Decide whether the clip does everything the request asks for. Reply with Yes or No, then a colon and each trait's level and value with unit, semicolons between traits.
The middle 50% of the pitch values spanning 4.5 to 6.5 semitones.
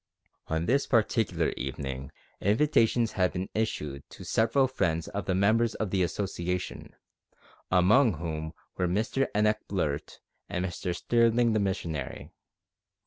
Yes: average, 4.9 semitones